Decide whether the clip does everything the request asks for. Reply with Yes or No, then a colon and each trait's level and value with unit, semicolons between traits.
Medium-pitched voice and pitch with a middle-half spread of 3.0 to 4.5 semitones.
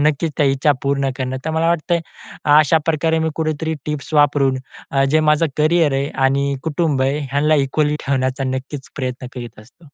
No: medium, 145 Hz; narrow, 2.5 semitones